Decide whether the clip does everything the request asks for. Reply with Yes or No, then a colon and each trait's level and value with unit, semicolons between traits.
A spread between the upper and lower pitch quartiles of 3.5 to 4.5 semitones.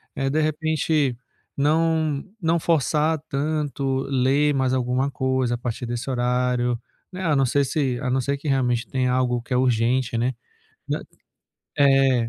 No: average, 2.9 semitones